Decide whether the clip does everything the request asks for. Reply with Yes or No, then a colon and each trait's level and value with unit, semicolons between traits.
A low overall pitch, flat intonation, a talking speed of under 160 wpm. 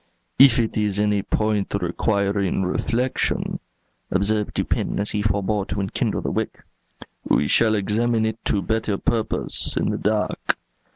Yes: low, 105 Hz; narrow, 1.9 semitones; average, 140 wpm